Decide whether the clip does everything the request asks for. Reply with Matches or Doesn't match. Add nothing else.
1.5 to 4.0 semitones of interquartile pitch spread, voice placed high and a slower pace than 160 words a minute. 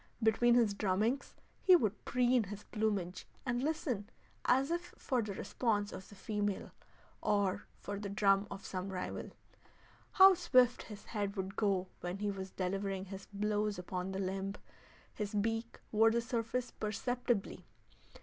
Matches